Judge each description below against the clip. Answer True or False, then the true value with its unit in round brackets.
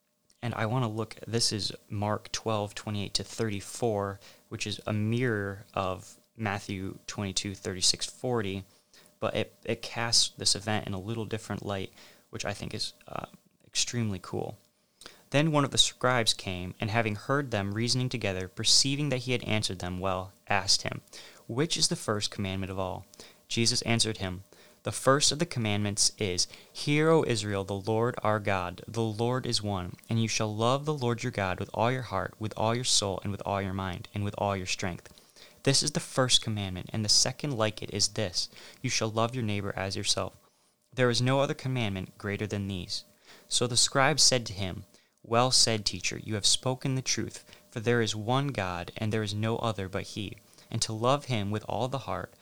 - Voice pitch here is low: True (110 Hz)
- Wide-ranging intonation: False (3.4 semitones)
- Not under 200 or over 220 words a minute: True (205 wpm)